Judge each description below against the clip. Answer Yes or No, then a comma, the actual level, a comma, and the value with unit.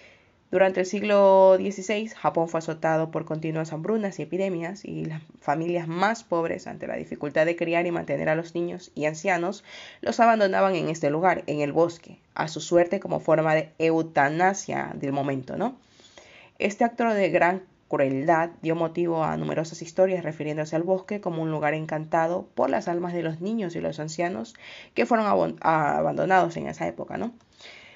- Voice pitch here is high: No, medium, 170 Hz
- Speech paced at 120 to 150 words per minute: No, average, 175 wpm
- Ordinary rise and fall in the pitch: Yes, average, 3.3 semitones